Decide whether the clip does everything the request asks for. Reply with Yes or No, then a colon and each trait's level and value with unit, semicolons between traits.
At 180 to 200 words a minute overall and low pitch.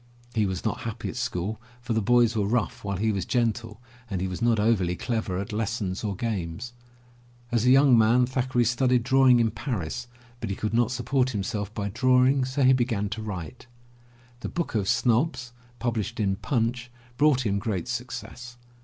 Yes: average, 185 wpm; low, 115 Hz